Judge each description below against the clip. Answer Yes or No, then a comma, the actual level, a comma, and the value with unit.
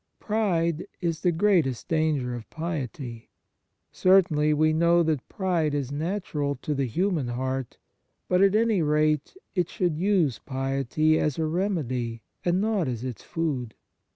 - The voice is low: No, medium, 155 Hz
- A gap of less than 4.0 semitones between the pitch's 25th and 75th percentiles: No, average, 4.9 semitones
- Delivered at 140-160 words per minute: Yes, average, 145 wpm